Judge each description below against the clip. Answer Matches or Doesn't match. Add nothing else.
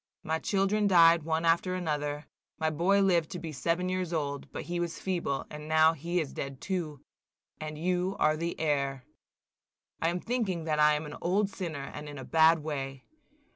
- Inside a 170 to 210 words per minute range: Matches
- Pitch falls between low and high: Matches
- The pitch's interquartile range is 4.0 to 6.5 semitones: Doesn't match